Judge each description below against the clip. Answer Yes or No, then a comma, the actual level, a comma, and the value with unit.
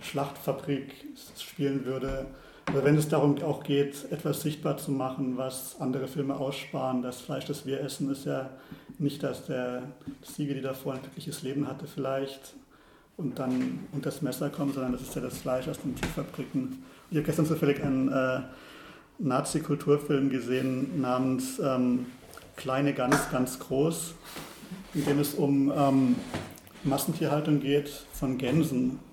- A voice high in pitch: No, medium, 140 Hz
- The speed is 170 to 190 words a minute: No, average, 150 wpm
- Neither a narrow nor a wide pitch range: No, narrow, 1.8 semitones